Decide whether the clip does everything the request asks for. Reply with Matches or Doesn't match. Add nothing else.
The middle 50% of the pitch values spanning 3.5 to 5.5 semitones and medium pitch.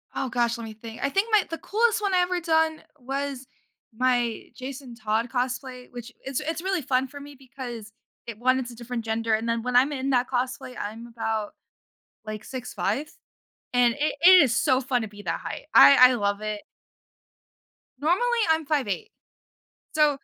Doesn't match